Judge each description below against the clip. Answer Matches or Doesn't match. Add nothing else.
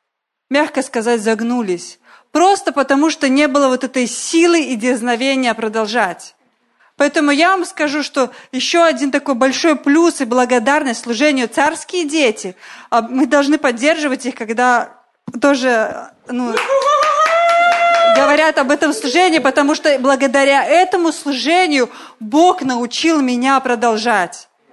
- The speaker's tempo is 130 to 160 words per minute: Doesn't match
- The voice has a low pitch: Doesn't match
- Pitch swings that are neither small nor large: Matches